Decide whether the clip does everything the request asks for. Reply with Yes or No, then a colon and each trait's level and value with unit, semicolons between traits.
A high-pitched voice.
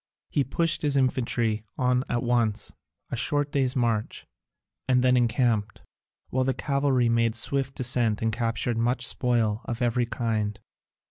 No: low, 120 Hz